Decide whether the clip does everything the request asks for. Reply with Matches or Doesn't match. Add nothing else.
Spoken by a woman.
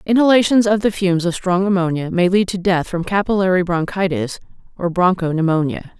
Matches